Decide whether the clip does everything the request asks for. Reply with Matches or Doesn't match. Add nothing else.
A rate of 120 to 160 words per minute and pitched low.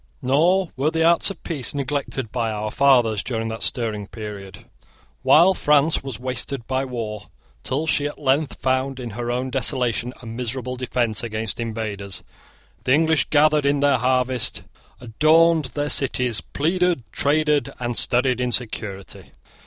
Matches